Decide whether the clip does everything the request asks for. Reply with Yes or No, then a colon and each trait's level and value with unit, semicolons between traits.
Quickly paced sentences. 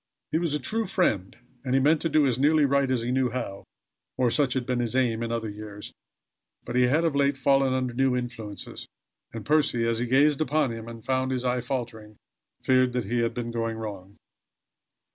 Yes: fast, 215 wpm